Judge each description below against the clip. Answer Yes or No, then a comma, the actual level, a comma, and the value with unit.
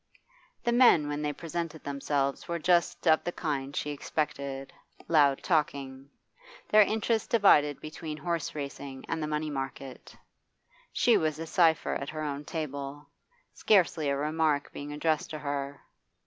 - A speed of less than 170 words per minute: Yes, average, 150 wpm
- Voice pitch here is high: No, medium, 150 Hz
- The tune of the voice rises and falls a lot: No, narrow, 2.5 semitones